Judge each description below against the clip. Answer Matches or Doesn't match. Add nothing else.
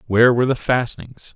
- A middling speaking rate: Matches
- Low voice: Matches